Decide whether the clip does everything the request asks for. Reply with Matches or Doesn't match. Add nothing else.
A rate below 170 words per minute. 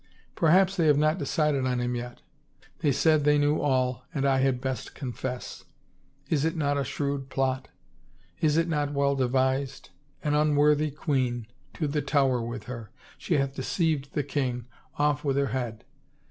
Doesn't match